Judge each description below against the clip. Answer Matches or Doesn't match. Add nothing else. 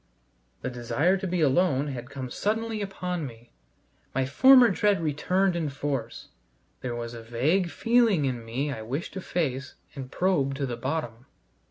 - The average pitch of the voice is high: Doesn't match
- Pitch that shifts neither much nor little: Doesn't match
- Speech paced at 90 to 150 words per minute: Doesn't match